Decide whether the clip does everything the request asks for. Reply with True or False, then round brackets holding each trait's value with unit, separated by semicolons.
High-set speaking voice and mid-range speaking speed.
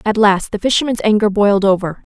True (205 Hz; 190 wpm)